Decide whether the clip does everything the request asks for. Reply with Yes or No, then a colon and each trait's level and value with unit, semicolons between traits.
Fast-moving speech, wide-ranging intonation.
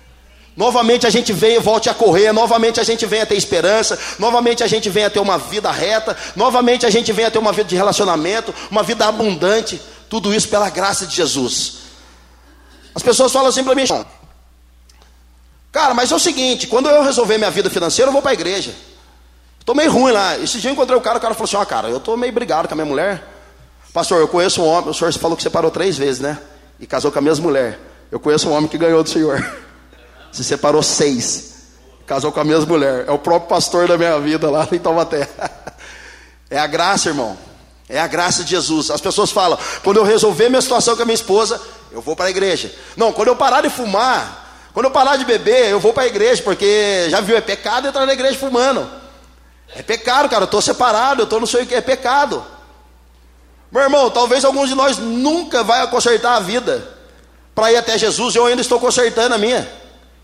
Yes: fast, 220 wpm; wide, 7.4 semitones